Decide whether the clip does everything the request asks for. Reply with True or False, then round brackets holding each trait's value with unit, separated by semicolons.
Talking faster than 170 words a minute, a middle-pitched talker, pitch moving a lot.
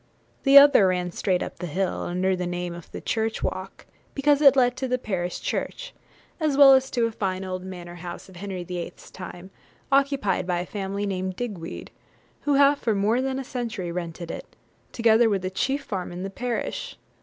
False (200 wpm; 195 Hz; 6.1 semitones)